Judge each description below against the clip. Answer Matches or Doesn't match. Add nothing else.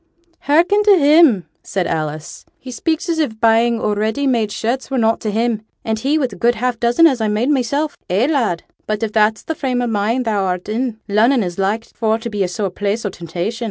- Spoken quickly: Matches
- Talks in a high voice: Matches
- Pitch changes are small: Doesn't match